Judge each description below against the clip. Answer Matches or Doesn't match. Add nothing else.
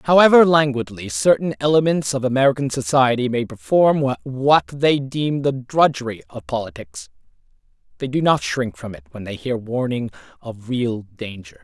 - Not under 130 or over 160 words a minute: Matches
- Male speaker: Matches